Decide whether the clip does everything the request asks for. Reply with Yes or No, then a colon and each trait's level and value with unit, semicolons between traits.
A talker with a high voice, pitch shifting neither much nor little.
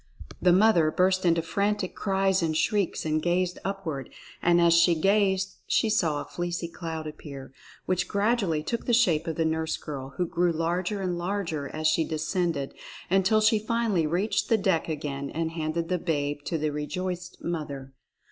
No: medium, 170 Hz; average, 3.5 semitones